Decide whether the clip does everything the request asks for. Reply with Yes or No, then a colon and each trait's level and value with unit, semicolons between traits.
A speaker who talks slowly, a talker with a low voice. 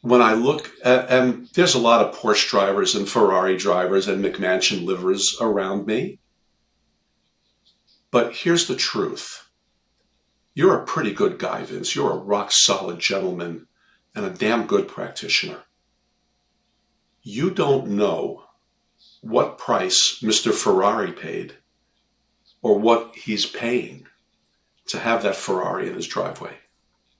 Yes: slow, 130 wpm; low, 105 Hz